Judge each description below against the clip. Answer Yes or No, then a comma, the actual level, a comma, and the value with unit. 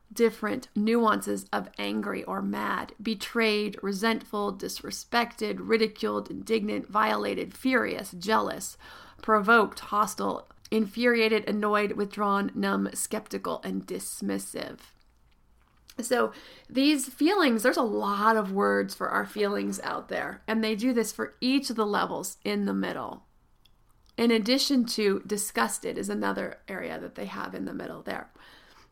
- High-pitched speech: Yes, high, 215 Hz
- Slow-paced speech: Yes, slow, 130 wpm